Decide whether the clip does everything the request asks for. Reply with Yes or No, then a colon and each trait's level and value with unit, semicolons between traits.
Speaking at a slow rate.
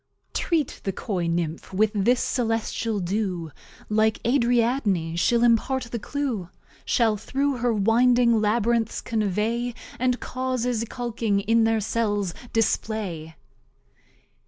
Yes: slow, 110 wpm